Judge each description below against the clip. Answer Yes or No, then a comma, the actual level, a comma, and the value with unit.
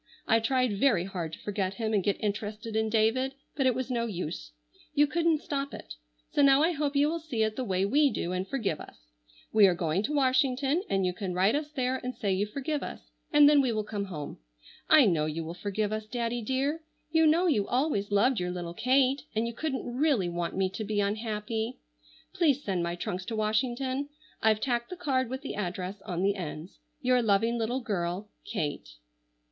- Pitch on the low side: No, high, 225 Hz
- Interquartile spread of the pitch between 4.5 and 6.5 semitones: Yes, wide, 5.5 semitones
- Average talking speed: No, fast, 210 wpm